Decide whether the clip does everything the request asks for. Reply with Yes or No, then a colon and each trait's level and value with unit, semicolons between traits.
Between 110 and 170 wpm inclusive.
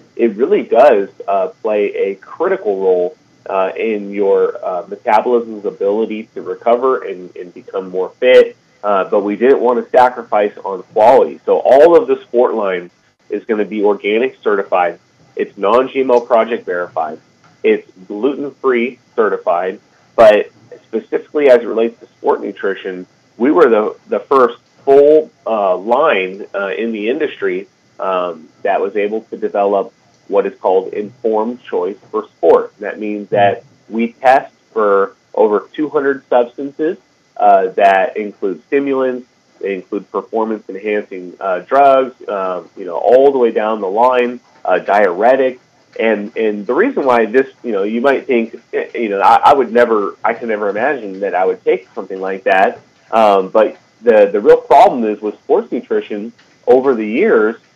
Yes: average, 160 wpm